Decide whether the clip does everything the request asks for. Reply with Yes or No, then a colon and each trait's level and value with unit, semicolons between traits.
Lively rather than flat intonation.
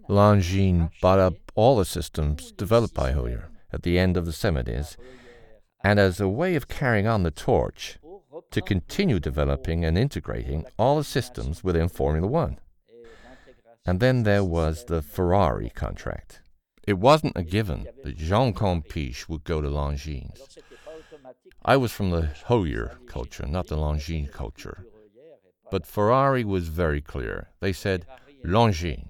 Yes: wide, 6.4 semitones